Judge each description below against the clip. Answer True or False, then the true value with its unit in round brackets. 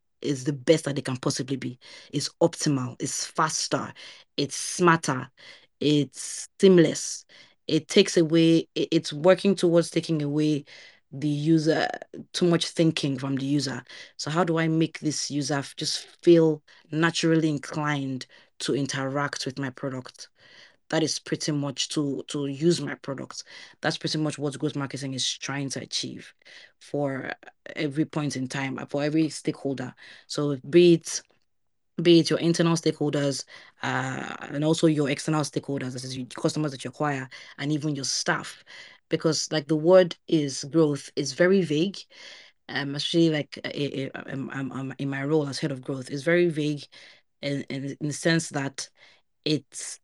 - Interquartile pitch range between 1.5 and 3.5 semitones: True (2.8 semitones)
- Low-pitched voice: False (150 Hz)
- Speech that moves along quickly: False (160 wpm)